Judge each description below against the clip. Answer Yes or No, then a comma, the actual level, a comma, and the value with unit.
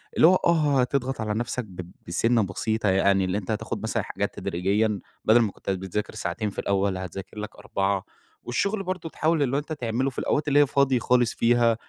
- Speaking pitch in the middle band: No, low, 115 Hz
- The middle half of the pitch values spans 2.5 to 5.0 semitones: No, wide, 5.6 semitones